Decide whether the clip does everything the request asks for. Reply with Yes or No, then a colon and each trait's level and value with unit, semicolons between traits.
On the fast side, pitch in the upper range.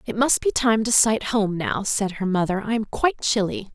Yes: fast, 240 wpm; high, 215 Hz